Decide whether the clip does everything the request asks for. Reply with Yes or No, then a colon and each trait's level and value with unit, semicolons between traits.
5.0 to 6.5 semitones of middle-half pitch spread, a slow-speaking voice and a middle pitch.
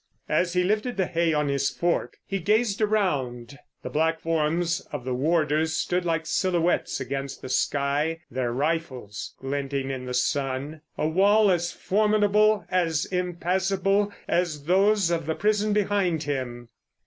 No: average, 5.3 semitones; average, 150 wpm; medium, 165 Hz